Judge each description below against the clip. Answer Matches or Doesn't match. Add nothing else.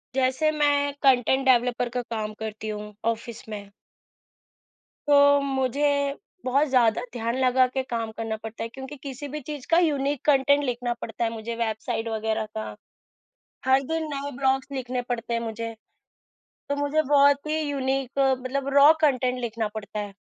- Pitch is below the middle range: Doesn't match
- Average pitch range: Matches